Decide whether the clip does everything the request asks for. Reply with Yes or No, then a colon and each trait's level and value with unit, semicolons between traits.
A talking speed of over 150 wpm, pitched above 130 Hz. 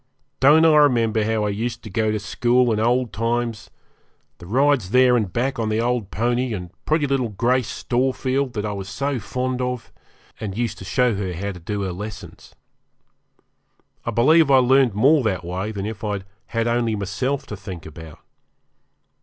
No: average, 185 wpm; low, 115 Hz